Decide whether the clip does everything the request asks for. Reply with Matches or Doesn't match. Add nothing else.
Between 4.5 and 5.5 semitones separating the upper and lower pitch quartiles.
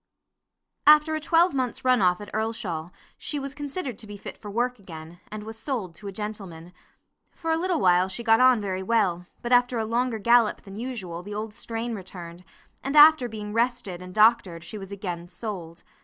Matches